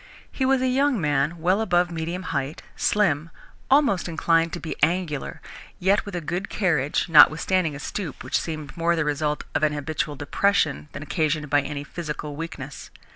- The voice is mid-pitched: Yes, medium, 165 Hz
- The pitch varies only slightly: No, average, 3.6 semitones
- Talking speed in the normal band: Yes, average, 175 wpm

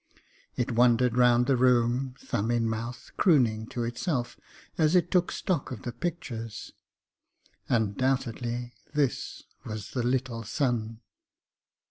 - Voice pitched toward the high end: No, low, 120 Hz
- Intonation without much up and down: Yes, narrow, 2.2 semitones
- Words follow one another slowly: Yes, slow, 120 wpm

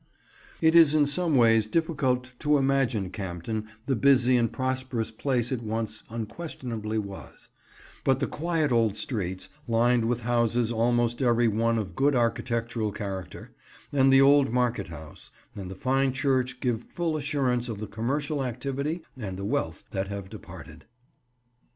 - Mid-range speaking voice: No, low, 120 Hz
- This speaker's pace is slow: No, average, 150 wpm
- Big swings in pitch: No, average, 3.7 semitones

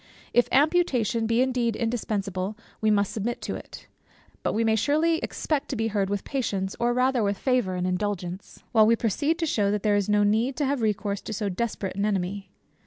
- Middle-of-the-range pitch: No, high, 220 Hz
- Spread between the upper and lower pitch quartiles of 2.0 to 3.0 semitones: No, average, 3.6 semitones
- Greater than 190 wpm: Yes, fast, 205 wpm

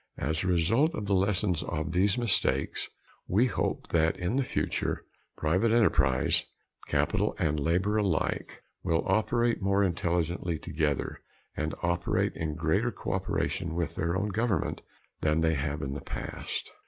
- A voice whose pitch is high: No, very low, 85 Hz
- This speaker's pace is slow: No, average, 150 wpm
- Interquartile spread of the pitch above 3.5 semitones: Yes, average, 4.2 semitones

